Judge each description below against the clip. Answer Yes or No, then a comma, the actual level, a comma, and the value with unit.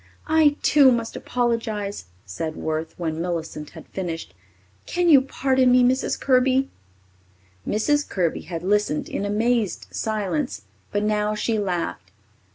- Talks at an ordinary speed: No, slow, 130 wpm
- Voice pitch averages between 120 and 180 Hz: No, high, 210 Hz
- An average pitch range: No, wide, 6.9 semitones